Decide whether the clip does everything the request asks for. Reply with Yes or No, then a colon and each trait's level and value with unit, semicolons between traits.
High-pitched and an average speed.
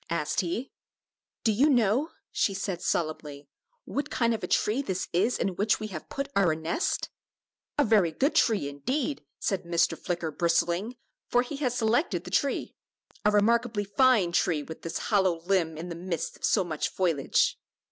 Yes: high, 195 Hz; average, 175 wpm